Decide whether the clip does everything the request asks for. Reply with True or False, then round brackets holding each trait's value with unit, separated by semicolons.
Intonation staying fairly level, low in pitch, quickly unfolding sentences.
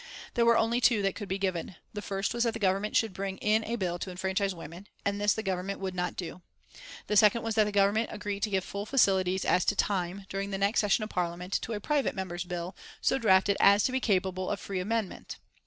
False (2.3 semitones; 200 Hz; 240 wpm)